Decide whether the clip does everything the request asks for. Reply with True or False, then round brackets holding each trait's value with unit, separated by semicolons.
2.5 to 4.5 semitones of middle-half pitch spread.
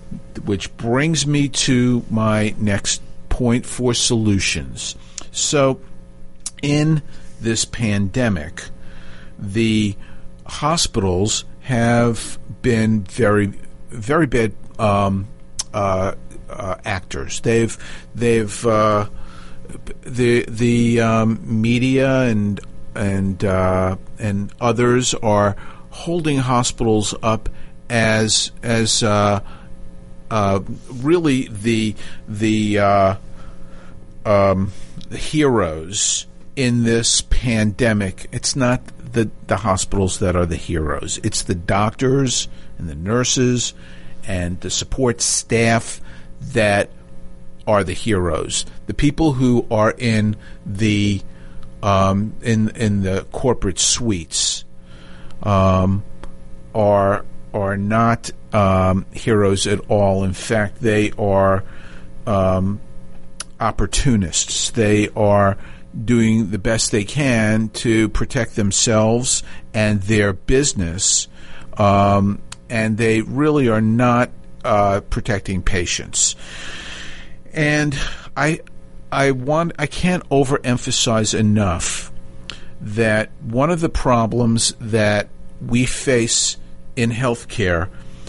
False (5.6 semitones)